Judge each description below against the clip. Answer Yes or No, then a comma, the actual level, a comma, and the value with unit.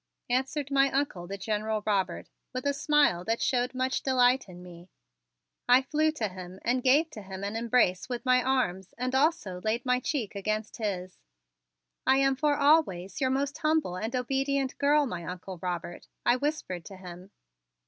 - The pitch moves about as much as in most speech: No, wide, 6.3 semitones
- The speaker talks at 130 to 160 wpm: No, average, 175 wpm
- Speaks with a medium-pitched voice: No, high, 245 Hz